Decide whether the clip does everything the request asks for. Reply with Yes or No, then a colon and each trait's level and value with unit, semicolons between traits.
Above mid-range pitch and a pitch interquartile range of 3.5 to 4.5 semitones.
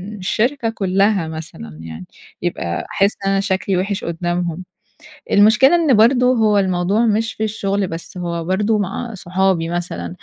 Yes: high, 195 Hz; average, 3.8 semitones